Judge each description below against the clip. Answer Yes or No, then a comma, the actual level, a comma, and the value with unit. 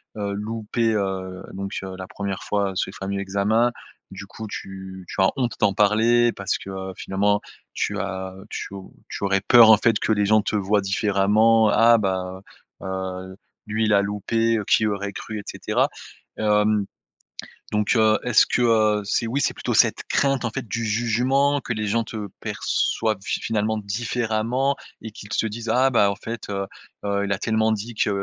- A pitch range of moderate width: No, narrow, 2.3 semitones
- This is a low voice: Yes, low, 105 Hz